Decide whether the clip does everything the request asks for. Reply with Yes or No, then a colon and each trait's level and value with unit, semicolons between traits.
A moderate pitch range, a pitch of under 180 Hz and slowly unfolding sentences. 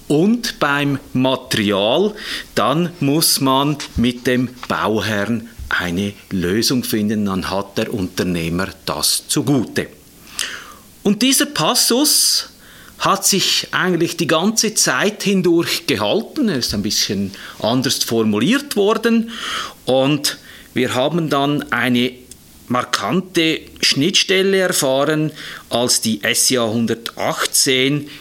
No: wide, 7.5 semitones; low, 135 Hz; slow, 100 wpm